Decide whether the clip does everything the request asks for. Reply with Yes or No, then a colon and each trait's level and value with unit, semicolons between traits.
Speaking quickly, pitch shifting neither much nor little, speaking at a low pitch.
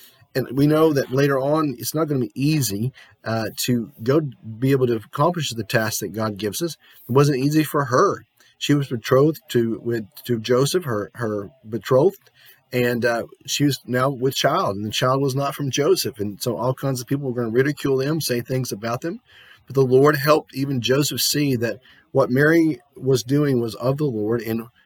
Yes: fast, 210 wpm; average, 3.4 semitones; low, 130 Hz